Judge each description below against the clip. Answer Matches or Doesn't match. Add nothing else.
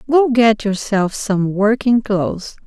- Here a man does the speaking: Doesn't match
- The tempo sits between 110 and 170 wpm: Matches